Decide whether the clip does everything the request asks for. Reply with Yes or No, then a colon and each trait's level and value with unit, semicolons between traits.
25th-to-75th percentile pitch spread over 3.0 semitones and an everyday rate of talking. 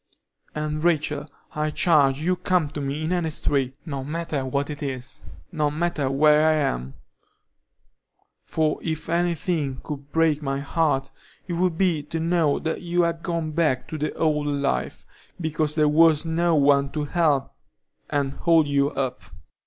No: narrow, 2.6 semitones; average, 170 wpm